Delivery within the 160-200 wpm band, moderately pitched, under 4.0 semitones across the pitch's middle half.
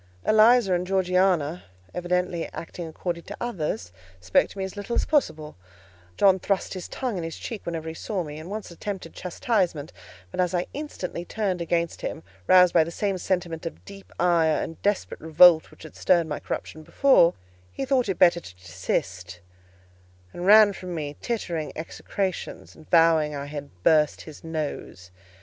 Yes: average, 170 wpm; medium, 175 Hz; average, 3.4 semitones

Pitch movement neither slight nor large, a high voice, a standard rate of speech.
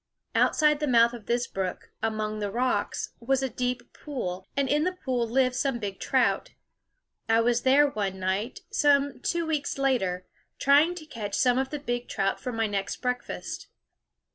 Yes: average, 4.4 semitones; high, 245 Hz; average, 175 wpm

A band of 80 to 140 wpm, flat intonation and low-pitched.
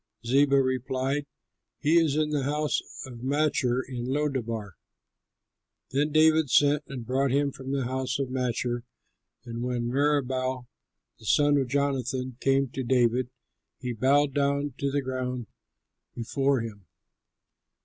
Yes: slow, 135 wpm; narrow, 2.2 semitones; low, 130 Hz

